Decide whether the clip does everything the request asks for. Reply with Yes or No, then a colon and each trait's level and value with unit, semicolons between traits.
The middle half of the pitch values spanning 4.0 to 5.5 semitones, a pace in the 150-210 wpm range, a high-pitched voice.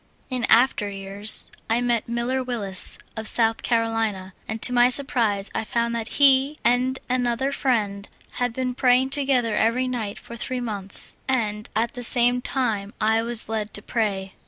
No: average, 2.7 semitones; average, 170 wpm; high, 235 Hz